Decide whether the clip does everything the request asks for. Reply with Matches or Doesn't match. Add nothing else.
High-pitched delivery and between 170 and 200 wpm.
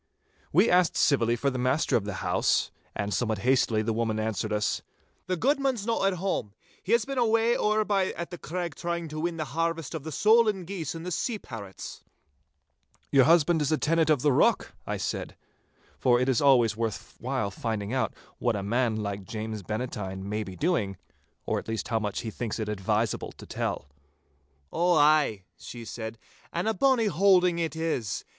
Doesn't match